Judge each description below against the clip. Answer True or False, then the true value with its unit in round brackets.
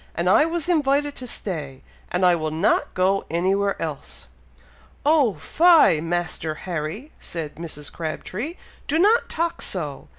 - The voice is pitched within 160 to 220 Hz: True (185 Hz)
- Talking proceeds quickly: False (140 wpm)